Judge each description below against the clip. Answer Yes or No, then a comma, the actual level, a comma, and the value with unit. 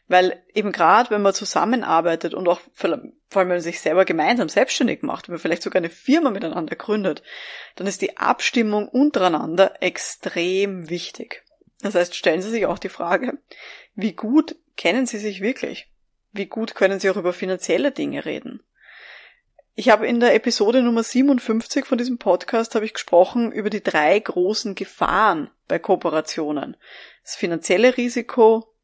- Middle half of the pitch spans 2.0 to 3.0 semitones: No, average, 4.7 semitones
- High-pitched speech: Yes, high, 210 Hz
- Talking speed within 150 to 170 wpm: Yes, average, 160 wpm